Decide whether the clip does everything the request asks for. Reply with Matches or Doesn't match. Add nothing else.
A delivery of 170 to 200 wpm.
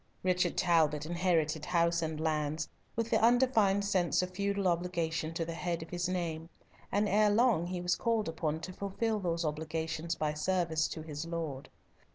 Matches